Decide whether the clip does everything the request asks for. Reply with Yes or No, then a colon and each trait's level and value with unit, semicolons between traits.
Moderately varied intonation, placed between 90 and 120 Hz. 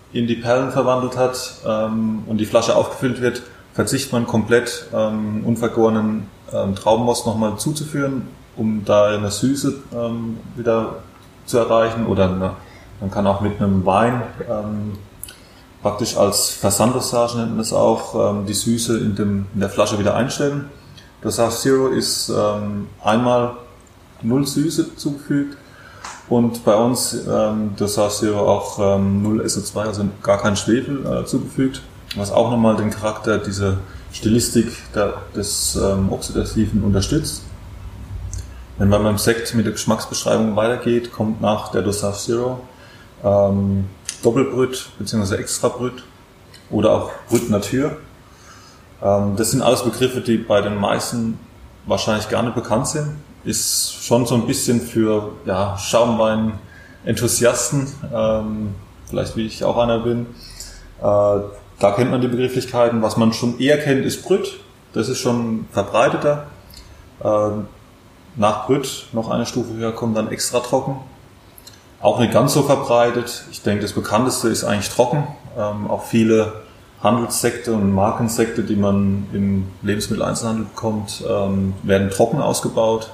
Yes: average, 3.1 semitones; low, 110 Hz